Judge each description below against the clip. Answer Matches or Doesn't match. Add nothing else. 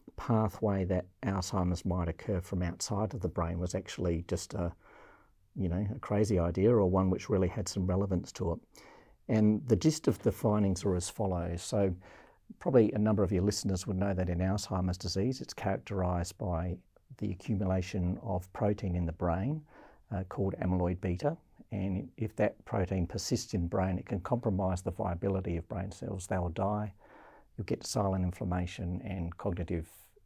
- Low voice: Matches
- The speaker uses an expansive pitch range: Doesn't match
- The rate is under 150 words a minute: Doesn't match